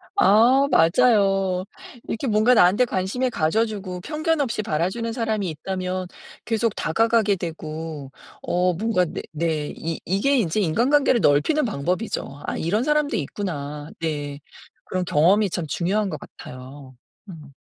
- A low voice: No, medium, 185 Hz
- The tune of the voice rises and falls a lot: Yes, wide, 6.1 semitones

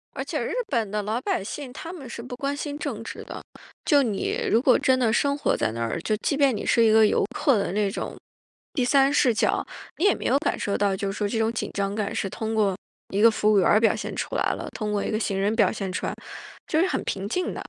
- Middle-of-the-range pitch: No, high, 220 Hz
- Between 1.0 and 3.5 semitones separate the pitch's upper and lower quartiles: No, average, 4.8 semitones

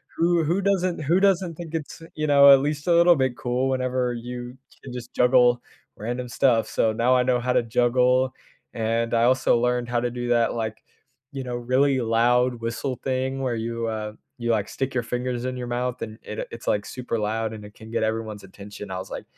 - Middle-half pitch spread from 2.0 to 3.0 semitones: Yes, narrow, 2.4 semitones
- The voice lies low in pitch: Yes, low, 125 Hz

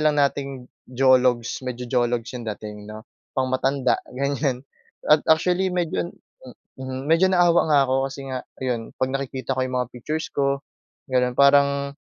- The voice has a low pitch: Yes, low, 130 Hz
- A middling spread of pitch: No, narrow, 2.2 semitones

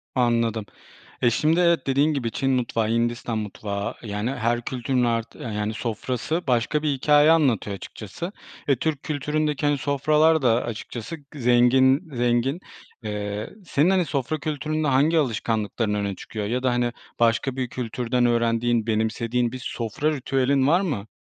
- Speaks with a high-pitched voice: No, low, 125 Hz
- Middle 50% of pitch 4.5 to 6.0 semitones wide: No, average, 4.0 semitones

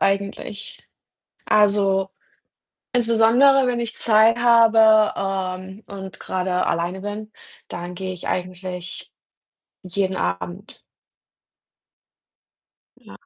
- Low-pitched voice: No, high, 195 Hz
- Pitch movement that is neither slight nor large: Yes, average, 3.2 semitones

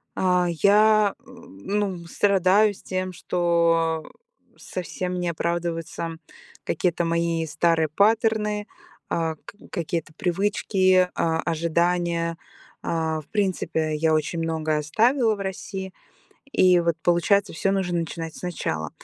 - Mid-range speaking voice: Yes, medium, 175 Hz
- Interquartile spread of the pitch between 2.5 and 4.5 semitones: Yes, average, 2.8 semitones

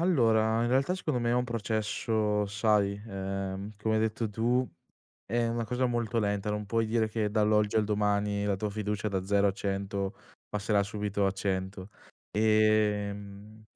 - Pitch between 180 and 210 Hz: No, low, 105 Hz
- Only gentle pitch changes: Yes, narrow, 1.8 semitones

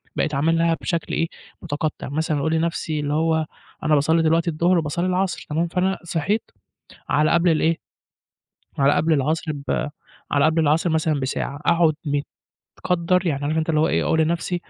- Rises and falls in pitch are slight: Yes, narrow, 1.8 semitones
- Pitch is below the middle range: No, medium, 160 Hz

